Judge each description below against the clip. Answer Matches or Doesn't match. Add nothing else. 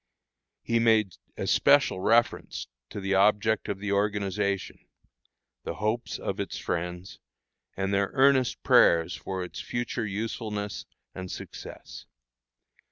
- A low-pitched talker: Matches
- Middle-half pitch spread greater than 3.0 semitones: Doesn't match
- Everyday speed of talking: Doesn't match